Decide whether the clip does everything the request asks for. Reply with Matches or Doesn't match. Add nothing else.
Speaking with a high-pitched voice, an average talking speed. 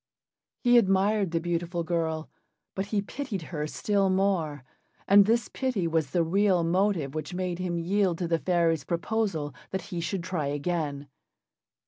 Doesn't match